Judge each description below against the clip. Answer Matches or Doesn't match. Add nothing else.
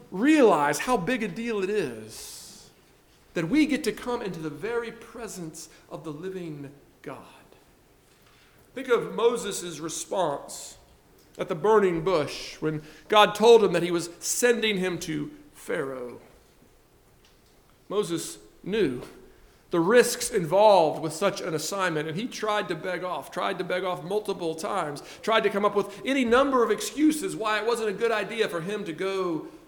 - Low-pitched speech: Doesn't match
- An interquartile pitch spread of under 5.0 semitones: Doesn't match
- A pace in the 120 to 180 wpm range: Matches